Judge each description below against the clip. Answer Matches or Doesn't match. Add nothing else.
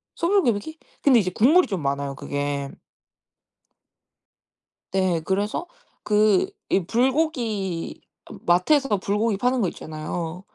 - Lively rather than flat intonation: Matches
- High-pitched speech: Matches